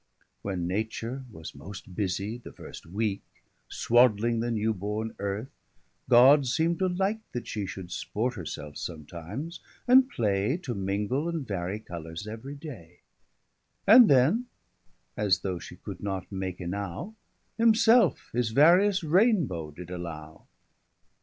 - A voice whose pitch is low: Yes, low, 110 Hz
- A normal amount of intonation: No, wide, 7.4 semitones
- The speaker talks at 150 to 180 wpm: No, average, 140 wpm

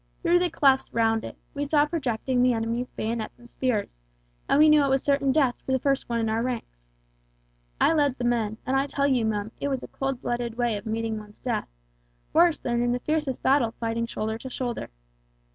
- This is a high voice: Yes, high, 245 Hz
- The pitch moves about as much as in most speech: Yes, average, 3.5 semitones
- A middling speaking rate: No, fast, 215 wpm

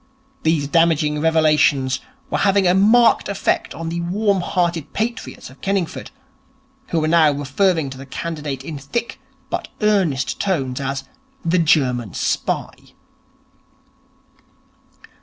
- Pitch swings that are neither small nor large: Yes, average, 4.9 semitones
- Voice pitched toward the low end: No, medium, 160 Hz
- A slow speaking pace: Yes, slow, 120 wpm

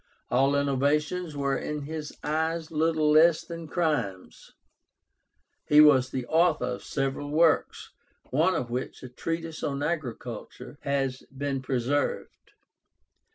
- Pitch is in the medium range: Yes, medium, 145 Hz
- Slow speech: Yes, slow, 120 wpm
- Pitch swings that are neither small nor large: Yes, average, 3.1 semitones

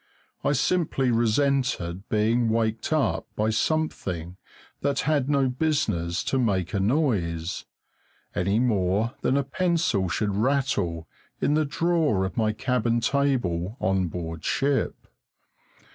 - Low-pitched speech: Yes, low, 115 Hz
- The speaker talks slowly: Yes, slow, 125 wpm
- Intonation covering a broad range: Yes, wide, 6.8 semitones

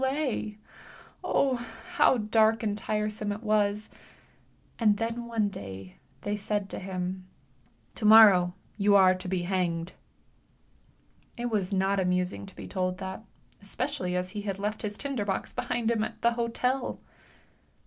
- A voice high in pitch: Yes, high, 205 Hz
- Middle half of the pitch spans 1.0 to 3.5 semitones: Yes, average, 3.1 semitones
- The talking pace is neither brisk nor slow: Yes, average, 145 wpm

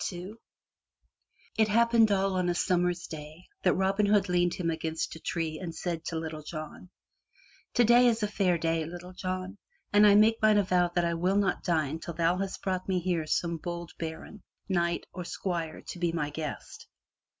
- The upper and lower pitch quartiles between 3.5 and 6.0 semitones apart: No, average, 2.9 semitones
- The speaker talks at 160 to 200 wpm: Yes, average, 185 wpm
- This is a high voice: No, medium, 175 Hz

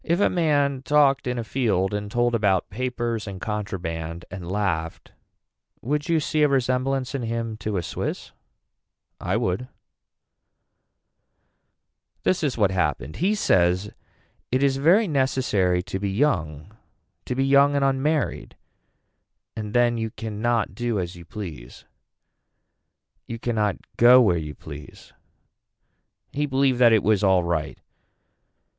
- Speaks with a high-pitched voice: No, low, 115 Hz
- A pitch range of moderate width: No, wide, 6.1 semitones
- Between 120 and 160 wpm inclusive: Yes, average, 140 wpm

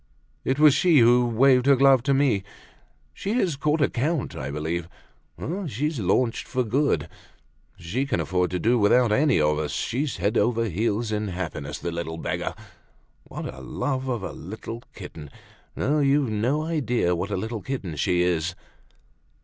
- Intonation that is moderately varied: No, wide, 7.4 semitones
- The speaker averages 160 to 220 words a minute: Yes, average, 175 wpm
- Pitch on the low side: Yes, low, 115 Hz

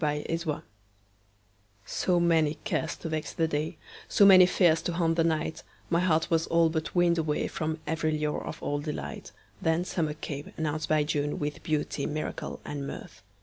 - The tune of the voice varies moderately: No, narrow, 1.8 semitones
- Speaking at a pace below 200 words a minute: Yes, average, 155 wpm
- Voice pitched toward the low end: No, medium, 160 Hz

